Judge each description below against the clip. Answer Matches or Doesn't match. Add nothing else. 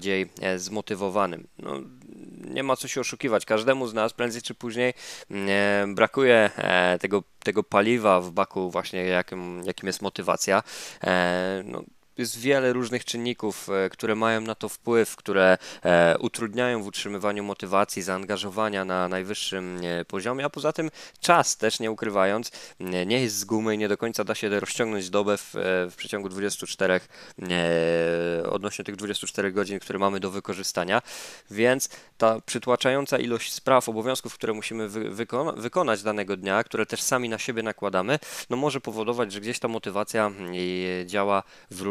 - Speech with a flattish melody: Doesn't match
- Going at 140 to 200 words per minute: Matches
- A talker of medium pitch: Doesn't match